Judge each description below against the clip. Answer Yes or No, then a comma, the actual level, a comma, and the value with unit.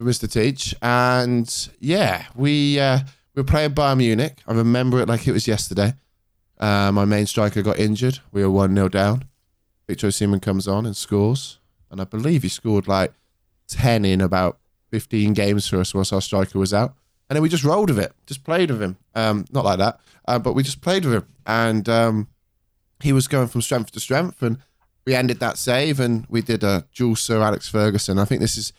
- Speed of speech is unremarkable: No, fast, 210 wpm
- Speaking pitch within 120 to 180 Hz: No, low, 110 Hz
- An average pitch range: Yes, average, 4.2 semitones